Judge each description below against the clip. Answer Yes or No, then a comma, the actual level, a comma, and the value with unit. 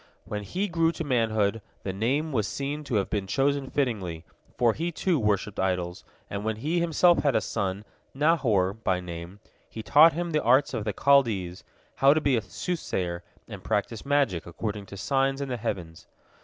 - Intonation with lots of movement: Yes, wide, 6.4 semitones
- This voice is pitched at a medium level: No, low, 115 Hz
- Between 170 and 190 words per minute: Yes, average, 185 wpm